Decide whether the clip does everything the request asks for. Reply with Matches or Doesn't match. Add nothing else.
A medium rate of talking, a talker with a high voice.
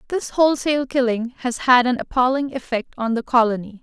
Matches